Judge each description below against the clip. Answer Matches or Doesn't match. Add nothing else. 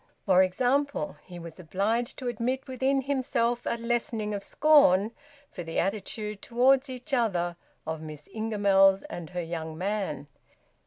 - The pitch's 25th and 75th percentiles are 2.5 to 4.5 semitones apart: Doesn't match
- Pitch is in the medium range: Doesn't match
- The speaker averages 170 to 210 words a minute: Doesn't match